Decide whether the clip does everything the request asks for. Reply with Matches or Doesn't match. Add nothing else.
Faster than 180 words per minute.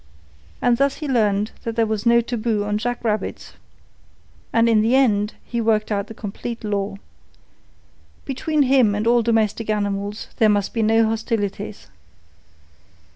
Doesn't match